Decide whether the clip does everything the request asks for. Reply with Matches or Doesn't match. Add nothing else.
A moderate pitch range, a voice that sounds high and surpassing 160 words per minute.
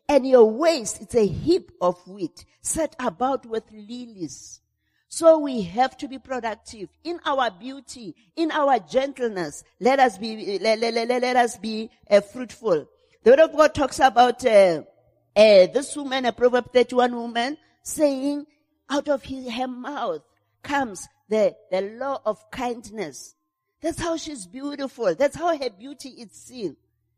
Doesn't match